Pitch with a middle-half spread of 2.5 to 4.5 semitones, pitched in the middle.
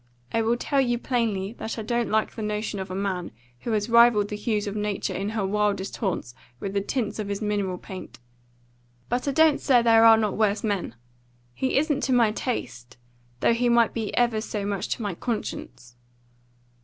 No: average, 2.9 semitones; high, 215 Hz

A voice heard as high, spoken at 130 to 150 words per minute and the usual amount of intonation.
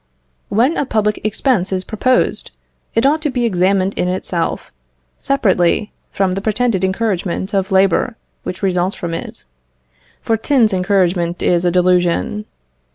Yes: high, 195 Hz; average, 140 wpm; average, 3.5 semitones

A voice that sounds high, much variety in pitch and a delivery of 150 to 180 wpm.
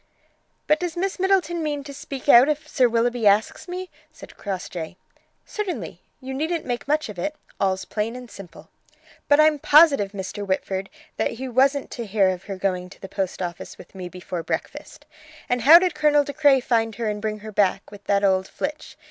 No: high, 235 Hz; wide, 7.3 semitones; average, 200 wpm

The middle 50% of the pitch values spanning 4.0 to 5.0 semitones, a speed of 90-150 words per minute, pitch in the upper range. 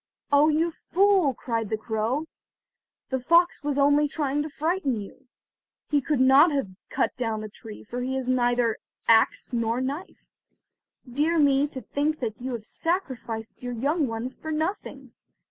No: average, 4.3 semitones; average, 165 wpm; very high, 265 Hz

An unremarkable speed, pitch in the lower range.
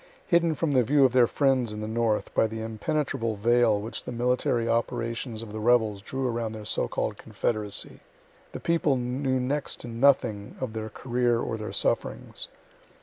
Yes: average, 180 wpm; low, 120 Hz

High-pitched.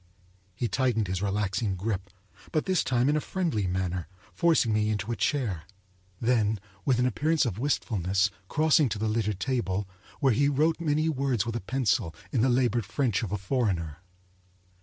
No: low, 115 Hz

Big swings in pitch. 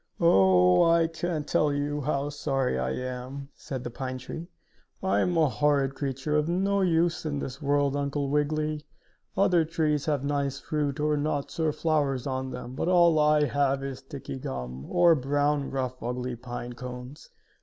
No: average, 2.8 semitones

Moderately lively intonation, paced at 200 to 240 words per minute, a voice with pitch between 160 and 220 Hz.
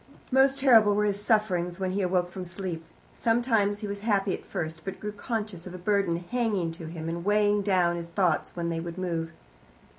Yes: average, 3.3 semitones; fast, 205 wpm; high, 190 Hz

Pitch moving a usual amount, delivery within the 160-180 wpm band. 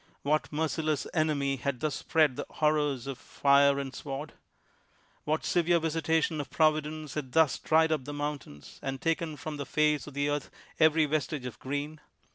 No: narrow, 2.0 semitones; average, 175 wpm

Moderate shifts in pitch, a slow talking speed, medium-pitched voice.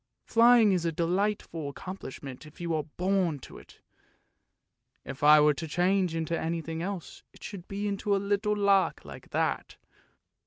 No: average, 3.7 semitones; average, 165 wpm; medium, 180 Hz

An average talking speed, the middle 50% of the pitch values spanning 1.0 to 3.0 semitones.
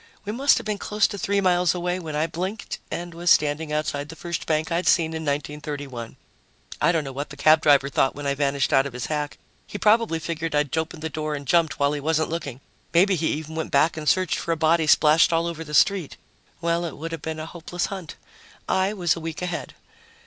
No: fast, 235 wpm; average, 2.7 semitones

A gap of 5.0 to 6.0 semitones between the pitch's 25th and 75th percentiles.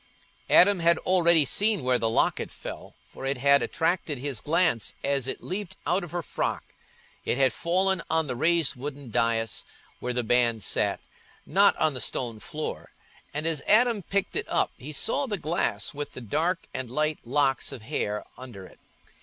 Yes: wide, 5.5 semitones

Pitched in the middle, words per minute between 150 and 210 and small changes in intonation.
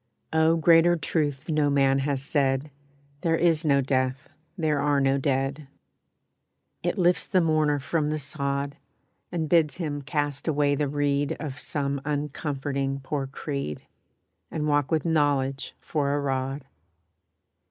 No: medium, 145 Hz; average, 140 wpm; narrow, 2.0 semitones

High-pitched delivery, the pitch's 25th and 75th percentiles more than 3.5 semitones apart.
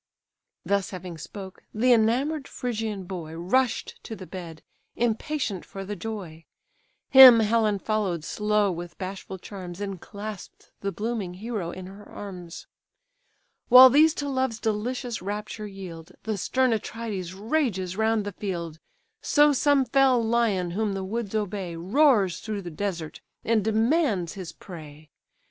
Yes: high, 205 Hz; average, 4.0 semitones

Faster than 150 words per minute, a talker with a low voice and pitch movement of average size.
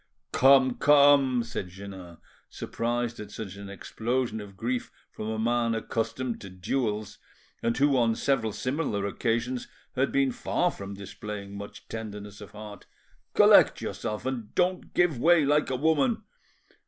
No: average, 145 wpm; low, 115 Hz; average, 4.1 semitones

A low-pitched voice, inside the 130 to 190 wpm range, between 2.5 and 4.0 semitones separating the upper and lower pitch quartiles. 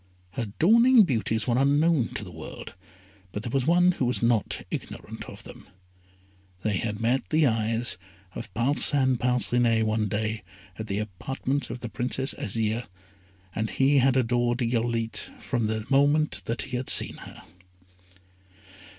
Yes: low, 120 Hz; average, 150 wpm; average, 3.4 semitones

